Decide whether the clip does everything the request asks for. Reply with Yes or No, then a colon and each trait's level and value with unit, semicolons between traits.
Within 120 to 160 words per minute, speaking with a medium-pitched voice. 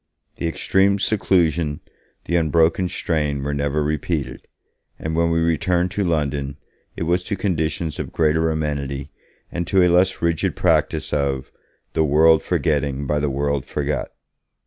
No: average, 145 wpm; very low, 80 Hz